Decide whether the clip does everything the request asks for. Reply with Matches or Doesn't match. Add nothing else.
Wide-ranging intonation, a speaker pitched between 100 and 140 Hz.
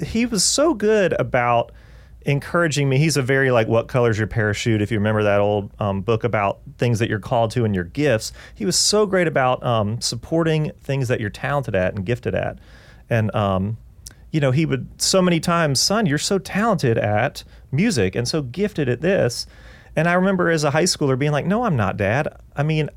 Matches